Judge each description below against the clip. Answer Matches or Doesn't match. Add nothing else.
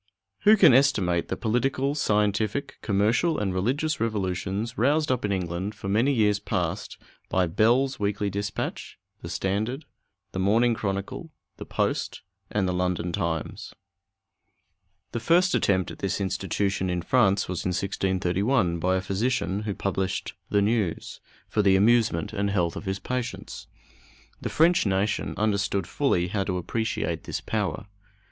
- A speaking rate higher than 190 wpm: Doesn't match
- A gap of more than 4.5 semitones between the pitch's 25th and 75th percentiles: Doesn't match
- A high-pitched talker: Doesn't match